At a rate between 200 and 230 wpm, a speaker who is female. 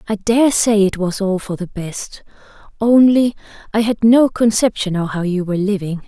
No: average, 190 wpm; female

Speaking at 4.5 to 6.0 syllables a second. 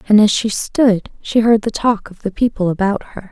Yes: 5.0 syllables/s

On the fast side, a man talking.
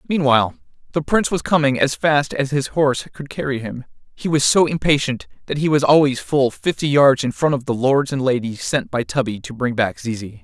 Yes: fast, 220 wpm; male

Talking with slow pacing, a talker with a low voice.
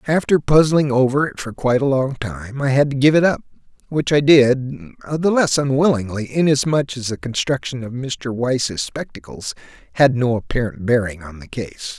No: average, 180 wpm; low, 130 Hz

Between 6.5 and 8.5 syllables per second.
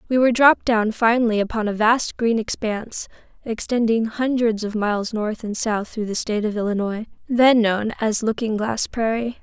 No: 5.2 syllables/s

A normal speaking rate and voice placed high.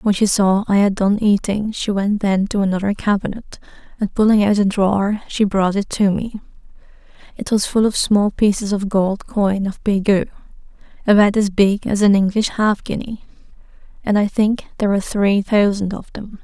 Yes: average, 185 wpm; high, 205 Hz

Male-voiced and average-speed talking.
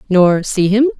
No: female; average, 180 wpm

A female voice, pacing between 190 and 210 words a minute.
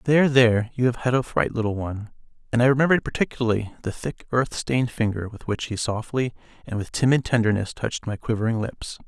No: male; average, 200 wpm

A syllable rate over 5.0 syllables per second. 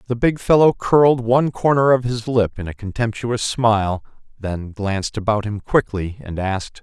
No: 4.9 syllables/s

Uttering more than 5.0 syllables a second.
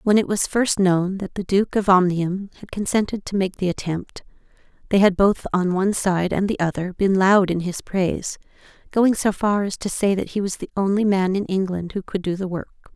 Yes: 5.2 syllables/s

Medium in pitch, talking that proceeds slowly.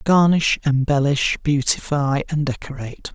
Yes: medium, 145 Hz; slow, 95 wpm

